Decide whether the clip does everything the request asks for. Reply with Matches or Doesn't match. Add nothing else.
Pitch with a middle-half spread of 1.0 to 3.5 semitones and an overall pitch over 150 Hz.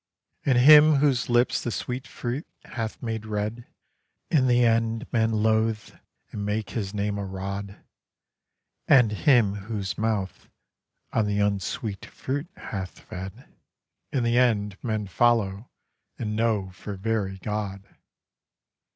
Doesn't match